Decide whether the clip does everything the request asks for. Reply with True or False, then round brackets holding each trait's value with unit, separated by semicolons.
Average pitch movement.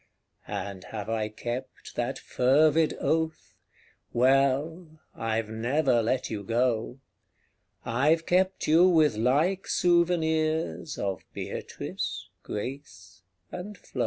False (6.0 semitones)